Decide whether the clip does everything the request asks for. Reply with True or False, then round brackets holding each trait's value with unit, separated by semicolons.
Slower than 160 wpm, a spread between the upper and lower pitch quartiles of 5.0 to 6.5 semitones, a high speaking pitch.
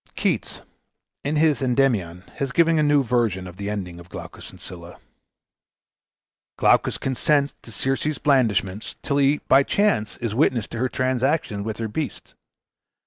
False (150 wpm; 5.5 semitones; 125 Hz)